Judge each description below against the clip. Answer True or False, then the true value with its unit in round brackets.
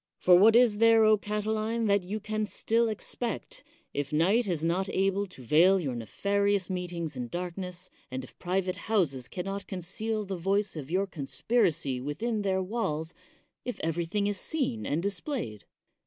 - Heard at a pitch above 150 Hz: True (190 Hz)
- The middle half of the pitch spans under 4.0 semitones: False (4.4 semitones)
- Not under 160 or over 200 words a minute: True (175 wpm)